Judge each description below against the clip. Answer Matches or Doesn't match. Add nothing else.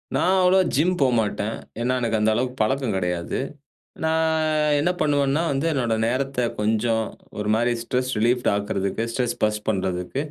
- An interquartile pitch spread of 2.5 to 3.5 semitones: Doesn't match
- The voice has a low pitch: Matches